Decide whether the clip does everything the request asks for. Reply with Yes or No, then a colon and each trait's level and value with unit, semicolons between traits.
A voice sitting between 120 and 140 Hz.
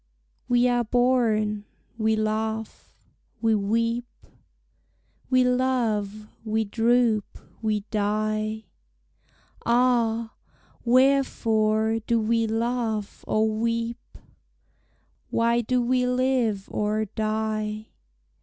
No: high, 225 Hz